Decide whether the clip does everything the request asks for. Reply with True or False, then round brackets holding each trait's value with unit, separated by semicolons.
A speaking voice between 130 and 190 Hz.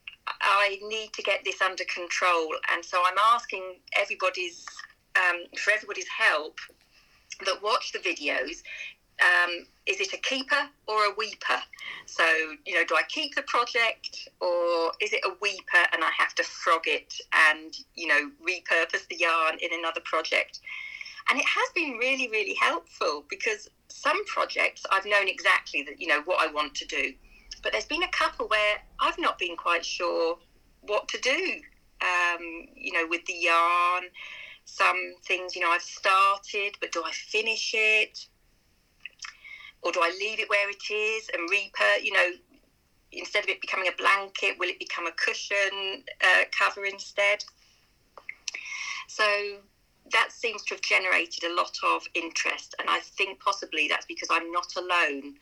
False (200 Hz)